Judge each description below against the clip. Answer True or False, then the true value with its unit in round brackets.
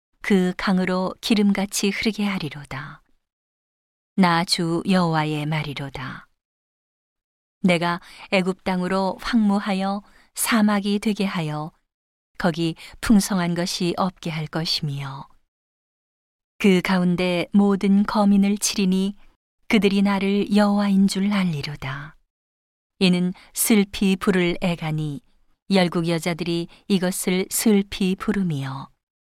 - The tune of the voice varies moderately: True (3.3 semitones)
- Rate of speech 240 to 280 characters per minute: False (215 characters per minute)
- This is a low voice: False (185 Hz)